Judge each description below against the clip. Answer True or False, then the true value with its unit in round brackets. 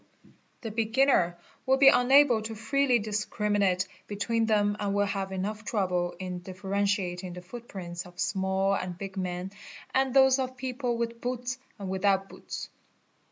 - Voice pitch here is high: True (205 Hz)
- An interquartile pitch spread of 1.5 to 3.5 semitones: False (4.1 semitones)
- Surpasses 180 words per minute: False (150 wpm)